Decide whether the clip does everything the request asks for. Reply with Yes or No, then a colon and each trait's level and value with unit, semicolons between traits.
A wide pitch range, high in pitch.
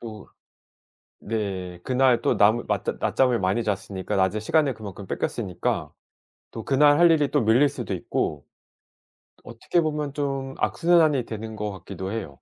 No: wide, 5.9 semitones; low, 115 Hz